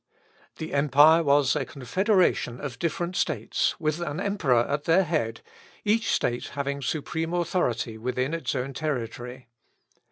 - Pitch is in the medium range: Yes, medium, 145 Hz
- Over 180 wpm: No, slow, 135 wpm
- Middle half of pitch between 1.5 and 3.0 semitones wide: No, average, 4.9 semitones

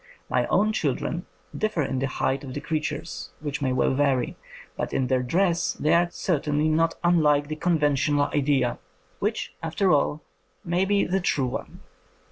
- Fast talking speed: No, average, 170 wpm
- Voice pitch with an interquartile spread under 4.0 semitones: Yes, average, 3.6 semitones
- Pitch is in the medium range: Yes, medium, 150 Hz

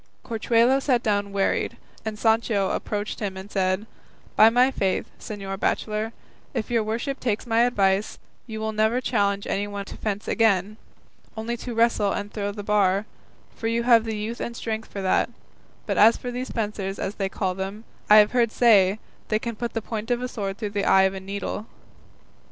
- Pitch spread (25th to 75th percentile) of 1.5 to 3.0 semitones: Yes, narrow, 2.4 semitones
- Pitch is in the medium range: No, high, 215 Hz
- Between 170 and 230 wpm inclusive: Yes, average, 190 wpm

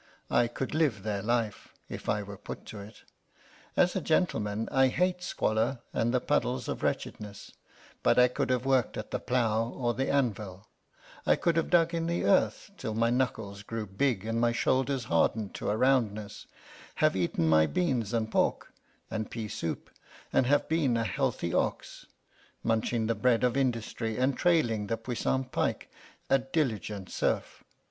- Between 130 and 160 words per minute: No, average, 170 wpm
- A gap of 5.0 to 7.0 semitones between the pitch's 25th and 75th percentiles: No, average, 3.8 semitones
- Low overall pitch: Yes, low, 115 Hz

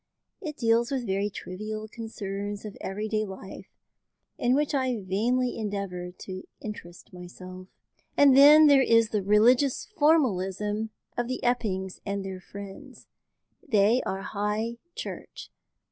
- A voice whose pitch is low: No, high, 215 Hz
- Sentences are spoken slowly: Yes, slow, 125 wpm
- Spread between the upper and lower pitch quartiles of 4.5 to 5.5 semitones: No, average, 4.0 semitones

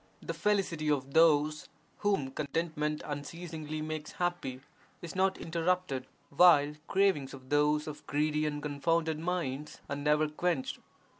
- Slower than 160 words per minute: Yes, slow, 135 wpm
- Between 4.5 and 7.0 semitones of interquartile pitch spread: No, narrow, 2.6 semitones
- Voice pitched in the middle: Yes, medium, 155 Hz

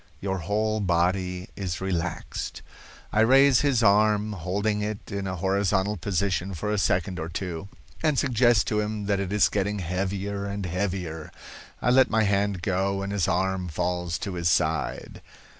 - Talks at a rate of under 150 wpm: No, average, 165 wpm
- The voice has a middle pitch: No, low, 100 Hz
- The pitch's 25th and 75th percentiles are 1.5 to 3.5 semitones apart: Yes, narrow, 2.4 semitones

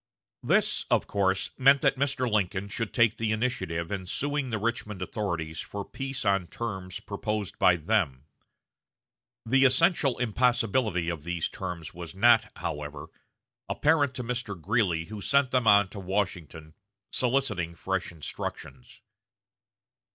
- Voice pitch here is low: Yes, low, 105 Hz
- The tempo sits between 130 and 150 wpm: Yes, slow, 135 wpm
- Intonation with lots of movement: Yes, wide, 5.7 semitones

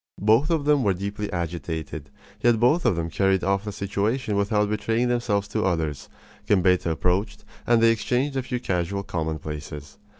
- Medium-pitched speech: No, low, 100 Hz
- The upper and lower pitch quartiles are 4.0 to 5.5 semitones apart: Yes, average, 4.8 semitones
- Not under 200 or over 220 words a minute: No, average, 165 wpm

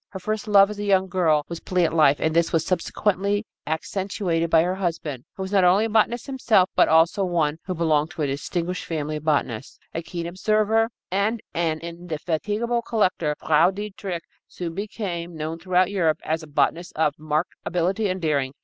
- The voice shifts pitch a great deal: No, average, 3.8 semitones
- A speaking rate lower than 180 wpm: No, average, 185 wpm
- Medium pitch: Yes, medium, 175 Hz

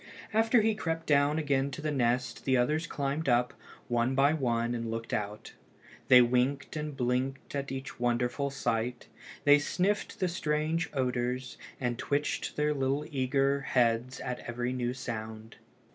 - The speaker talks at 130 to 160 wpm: Yes, average, 155 wpm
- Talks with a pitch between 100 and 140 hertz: Yes, low, 135 Hz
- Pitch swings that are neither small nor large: Yes, average, 3.2 semitones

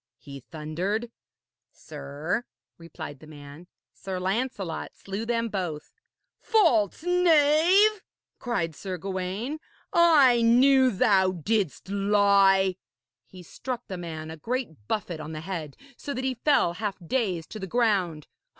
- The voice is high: Yes, high, 195 Hz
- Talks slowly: Yes, slow, 130 wpm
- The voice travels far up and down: Yes, wide, 6.4 semitones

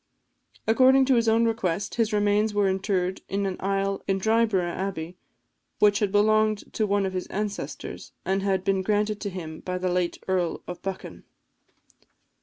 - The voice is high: Yes, high, 195 Hz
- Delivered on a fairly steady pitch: Yes, narrow, 2.2 semitones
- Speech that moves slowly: No, average, 170 wpm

